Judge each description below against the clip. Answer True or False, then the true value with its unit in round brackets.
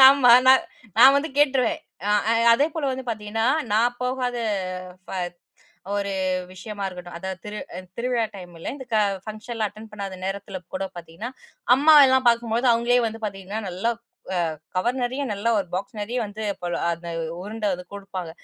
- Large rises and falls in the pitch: False (4.3 semitones)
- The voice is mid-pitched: False (220 Hz)